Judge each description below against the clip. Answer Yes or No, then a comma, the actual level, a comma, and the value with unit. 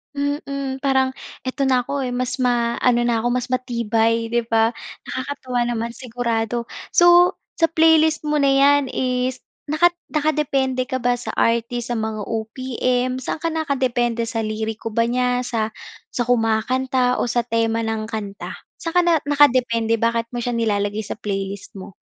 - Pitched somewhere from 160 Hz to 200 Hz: No, high, 245 Hz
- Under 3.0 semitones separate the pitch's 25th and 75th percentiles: Yes, narrow, 2.6 semitones